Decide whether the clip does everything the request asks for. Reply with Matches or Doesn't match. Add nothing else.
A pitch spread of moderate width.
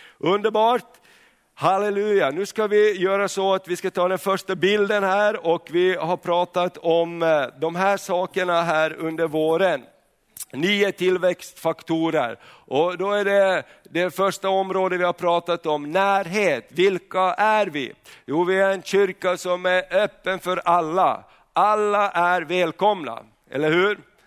Doesn't match